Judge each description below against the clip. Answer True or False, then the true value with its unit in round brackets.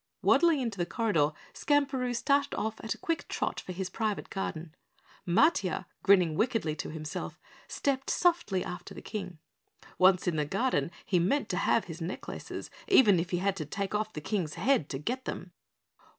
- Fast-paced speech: False (180 wpm)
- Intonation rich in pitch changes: True (6.4 semitones)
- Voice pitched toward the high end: True (195 Hz)